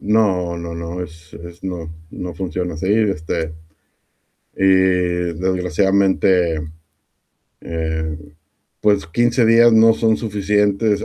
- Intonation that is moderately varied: Yes, average, 3.4 semitones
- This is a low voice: Yes, very low, 90 Hz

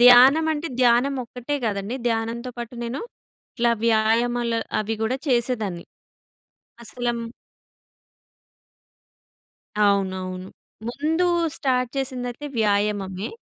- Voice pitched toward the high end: Yes, high, 235 Hz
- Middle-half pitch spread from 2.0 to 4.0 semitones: Yes, average, 2.7 semitones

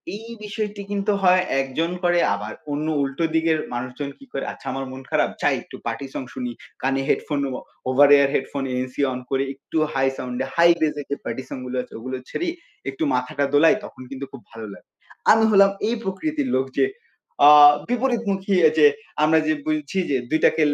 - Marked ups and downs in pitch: Yes, wide, 6.4 semitones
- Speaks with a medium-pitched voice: Yes, medium, 150 Hz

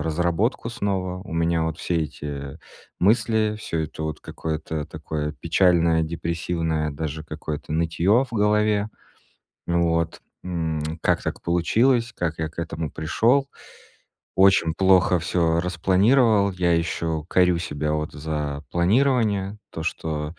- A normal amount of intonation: Yes, average, 3.6 semitones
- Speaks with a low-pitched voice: Yes, very low, 85 Hz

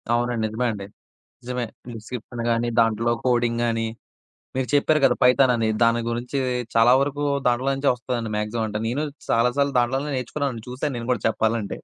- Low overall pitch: Yes, low, 120 Hz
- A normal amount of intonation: No, narrow, 2.0 semitones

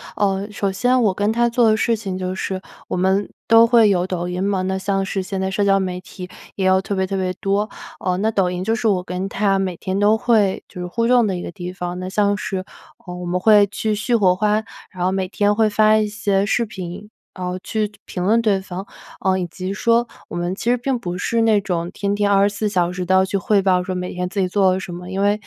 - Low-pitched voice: No, high, 195 Hz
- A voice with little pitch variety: Yes, narrow, 2.3 semitones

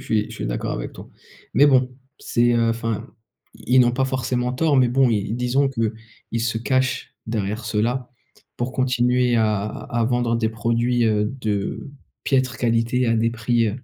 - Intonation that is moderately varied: No, narrow, 2.0 semitones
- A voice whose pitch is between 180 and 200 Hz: No, low, 120 Hz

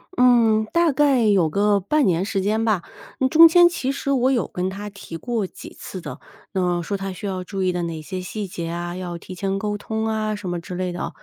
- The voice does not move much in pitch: No, average, 3.9 semitones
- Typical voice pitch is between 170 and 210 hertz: Yes, high, 200 Hz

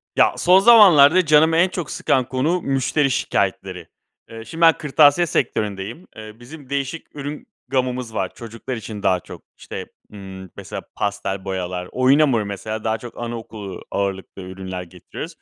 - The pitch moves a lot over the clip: Yes, wide, 6.9 semitones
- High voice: No, low, 120 Hz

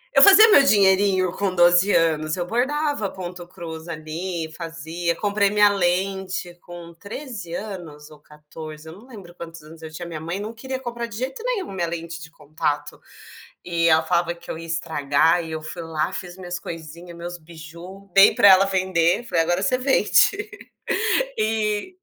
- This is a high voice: No, medium, 175 Hz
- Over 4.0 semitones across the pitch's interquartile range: No, average, 3.6 semitones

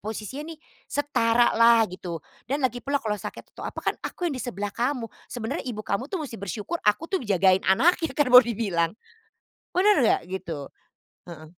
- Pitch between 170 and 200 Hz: No, high, 230 Hz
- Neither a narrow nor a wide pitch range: No, wide, 6.0 semitones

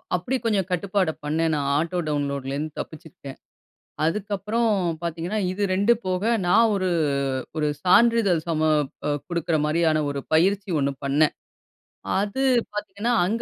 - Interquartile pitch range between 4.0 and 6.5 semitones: Yes, average, 4.6 semitones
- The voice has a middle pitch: Yes, medium, 180 Hz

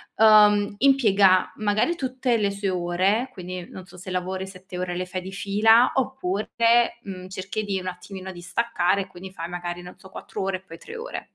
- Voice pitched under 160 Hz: No, high, 190 Hz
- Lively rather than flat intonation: No, average, 2.9 semitones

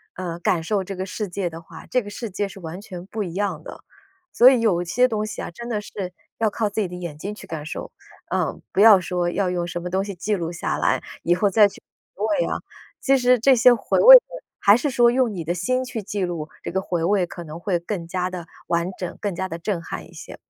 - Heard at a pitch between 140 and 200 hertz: Yes, high, 190 Hz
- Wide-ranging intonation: No, average, 3.8 semitones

